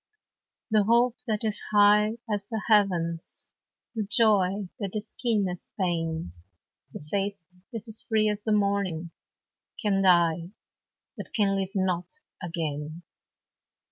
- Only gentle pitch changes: No, average, 3.5 semitones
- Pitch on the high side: Yes, high, 200 Hz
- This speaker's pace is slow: Yes, slow, 130 wpm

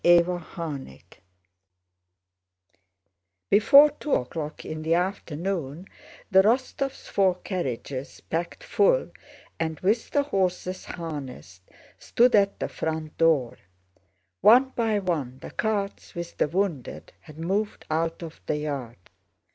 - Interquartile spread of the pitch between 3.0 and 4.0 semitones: No, average, 4.8 semitones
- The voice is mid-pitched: Yes, medium, 170 Hz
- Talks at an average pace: No, slow, 115 wpm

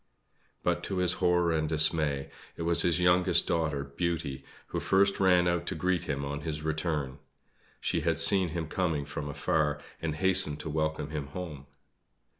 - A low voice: Yes, very low, 80 Hz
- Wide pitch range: No, average, 3.0 semitones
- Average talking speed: Yes, average, 170 wpm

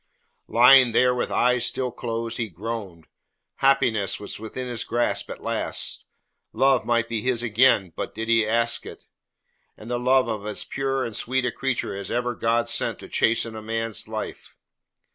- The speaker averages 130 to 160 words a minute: No, average, 175 wpm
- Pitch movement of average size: No, narrow, 2.0 semitones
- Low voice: Yes, low, 115 Hz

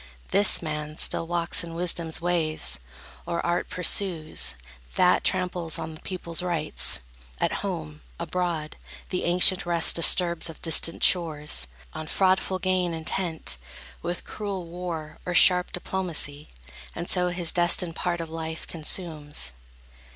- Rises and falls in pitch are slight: Yes, narrow, 2.2 semitones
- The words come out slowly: Yes, slow, 130 wpm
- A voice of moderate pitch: Yes, medium, 170 Hz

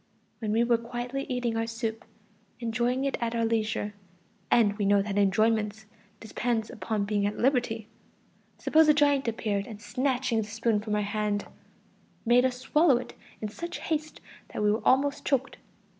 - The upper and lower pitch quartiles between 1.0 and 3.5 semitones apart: Yes, average, 3.0 semitones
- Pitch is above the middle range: Yes, high, 230 Hz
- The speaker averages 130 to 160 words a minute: No, average, 170 wpm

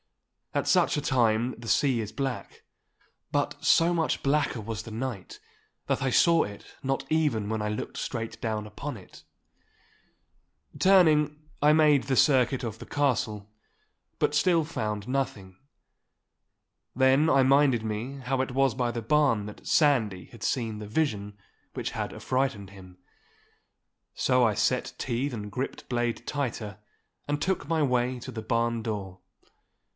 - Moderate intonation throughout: Yes, average, 4.5 semitones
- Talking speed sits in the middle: Yes, average, 150 wpm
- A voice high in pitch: No, low, 125 Hz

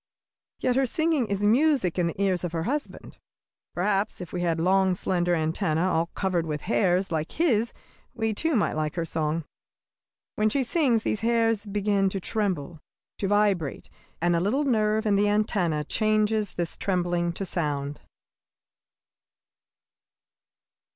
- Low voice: No, high, 195 Hz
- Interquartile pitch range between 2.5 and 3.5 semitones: No, average, 4.0 semitones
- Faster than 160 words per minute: No, average, 150 wpm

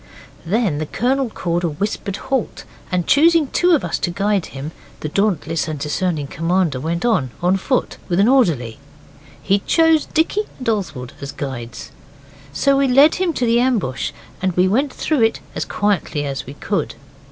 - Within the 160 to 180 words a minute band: Yes, average, 175 wpm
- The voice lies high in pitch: Yes, high, 195 Hz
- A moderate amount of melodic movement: No, wide, 8.5 semitones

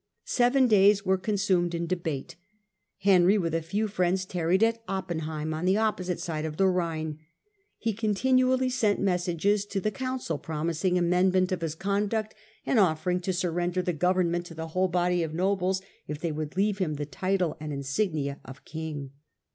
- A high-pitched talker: No, medium, 180 Hz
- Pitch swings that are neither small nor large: Yes, average, 3.4 semitones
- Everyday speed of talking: Yes, average, 170 wpm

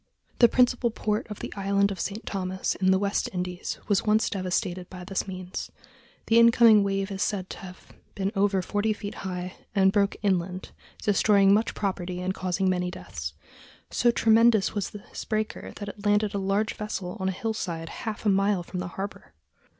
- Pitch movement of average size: No, narrow, 2.2 semitones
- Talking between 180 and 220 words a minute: Yes, average, 185 wpm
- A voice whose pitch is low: No, high, 195 Hz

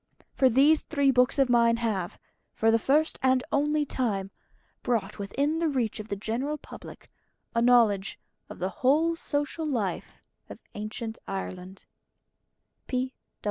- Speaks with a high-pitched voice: Yes, high, 245 Hz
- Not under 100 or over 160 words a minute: Yes, average, 140 wpm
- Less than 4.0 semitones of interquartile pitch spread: No, average, 5.1 semitones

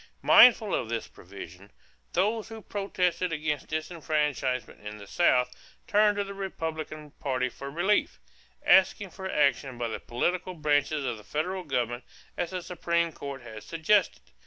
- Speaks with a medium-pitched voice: Yes, medium, 155 Hz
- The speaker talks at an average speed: Yes, average, 150 wpm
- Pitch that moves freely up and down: Yes, wide, 6.3 semitones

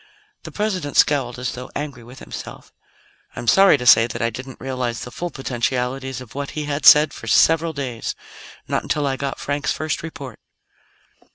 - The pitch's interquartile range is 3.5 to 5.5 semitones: No, average, 3.1 semitones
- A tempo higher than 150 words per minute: Yes, average, 180 wpm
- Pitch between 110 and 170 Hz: Yes, low, 135 Hz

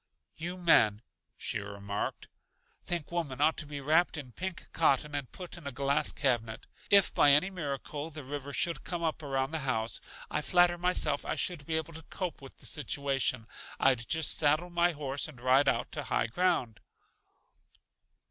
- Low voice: No, medium, 145 Hz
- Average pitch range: Yes, average, 4.0 semitones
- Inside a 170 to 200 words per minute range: Yes, average, 175 wpm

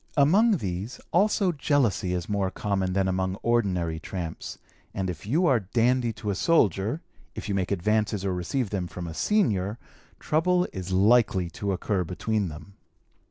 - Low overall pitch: Yes, low, 100 Hz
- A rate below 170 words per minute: Yes, average, 160 wpm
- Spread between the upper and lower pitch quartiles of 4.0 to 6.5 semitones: Yes, average, 4.9 semitones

